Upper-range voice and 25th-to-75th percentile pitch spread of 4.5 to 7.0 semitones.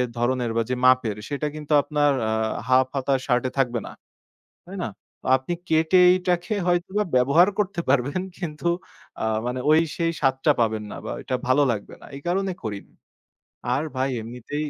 No: medium, 140 Hz; wide, 5.4 semitones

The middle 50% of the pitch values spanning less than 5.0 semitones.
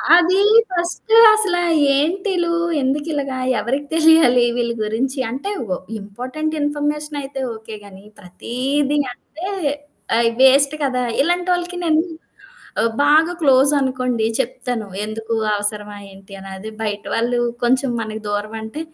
No: wide, 5.6 semitones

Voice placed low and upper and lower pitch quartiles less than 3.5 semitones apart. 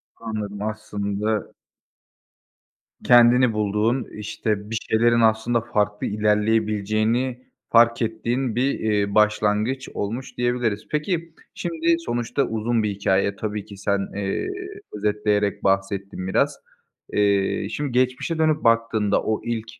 Yes: low, 110 Hz; average, 2.7 semitones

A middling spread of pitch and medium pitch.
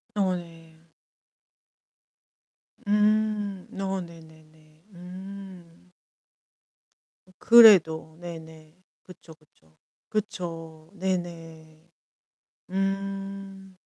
Yes: average, 3.3 semitones; medium, 180 Hz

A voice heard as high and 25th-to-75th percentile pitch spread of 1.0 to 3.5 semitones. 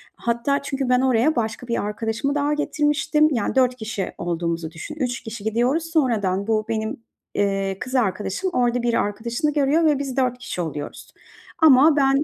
No: high, 245 Hz; average, 4.7 semitones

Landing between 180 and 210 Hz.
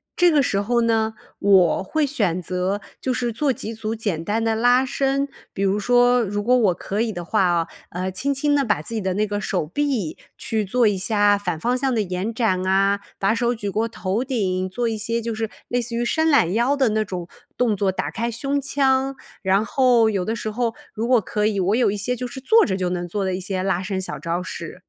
No: high, 220 Hz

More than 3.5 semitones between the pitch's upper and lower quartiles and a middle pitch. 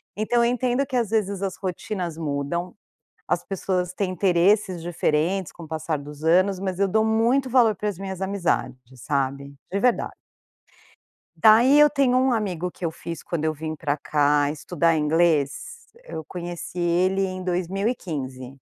Yes: average, 4.8 semitones; medium, 180 Hz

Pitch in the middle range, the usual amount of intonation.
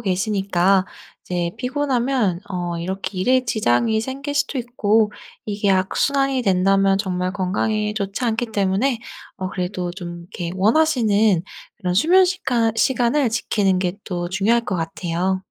No: high, 205 Hz; average, 4.4 semitones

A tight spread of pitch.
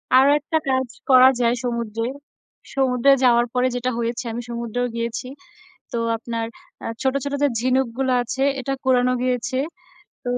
Yes: narrow, 1.7 semitones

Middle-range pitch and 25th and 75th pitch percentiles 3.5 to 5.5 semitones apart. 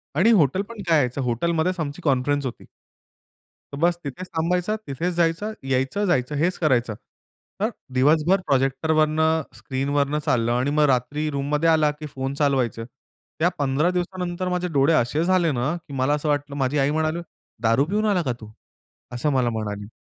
Yes: medium, 150 Hz; average, 4.2 semitones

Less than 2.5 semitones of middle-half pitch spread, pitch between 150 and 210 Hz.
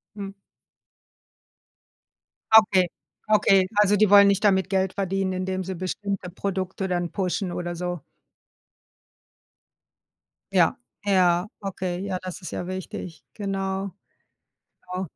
Yes: narrow, 1.5 semitones; high, 190 Hz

